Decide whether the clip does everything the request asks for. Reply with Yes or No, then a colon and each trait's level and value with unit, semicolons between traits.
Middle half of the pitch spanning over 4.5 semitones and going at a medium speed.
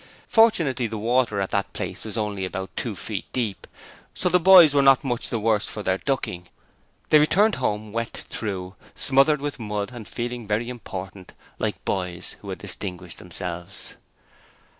Yes: wide, 5.6 semitones; average, 165 wpm